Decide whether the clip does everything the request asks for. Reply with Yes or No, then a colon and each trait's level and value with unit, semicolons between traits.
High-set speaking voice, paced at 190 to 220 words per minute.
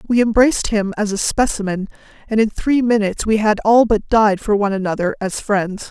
Yes: high, 210 Hz; fast, 205 wpm